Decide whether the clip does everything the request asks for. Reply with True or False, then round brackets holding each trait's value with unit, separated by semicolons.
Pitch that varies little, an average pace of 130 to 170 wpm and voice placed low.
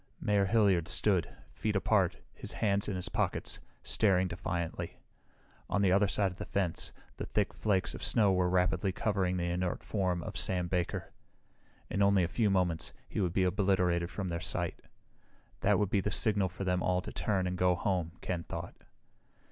False (1.9 semitones; 185 wpm; 95 Hz)